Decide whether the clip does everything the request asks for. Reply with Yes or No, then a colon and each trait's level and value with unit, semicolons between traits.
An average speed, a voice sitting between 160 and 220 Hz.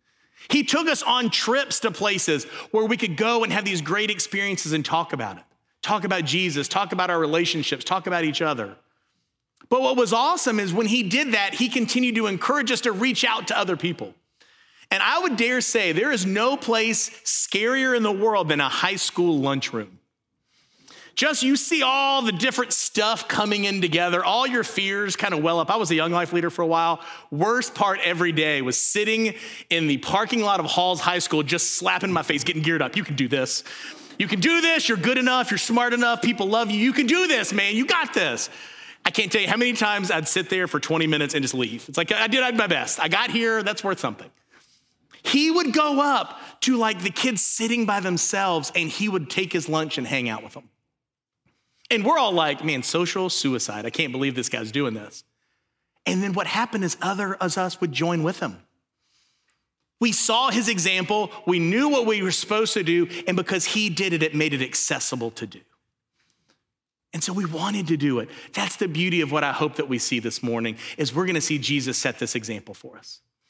No: fast, 220 wpm; high, 190 Hz